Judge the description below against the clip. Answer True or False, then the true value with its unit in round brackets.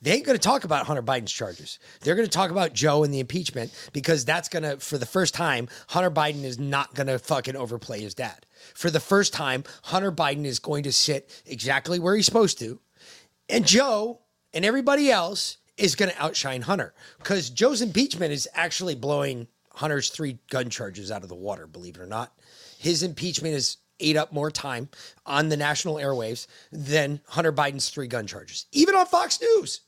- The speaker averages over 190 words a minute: True (200 wpm)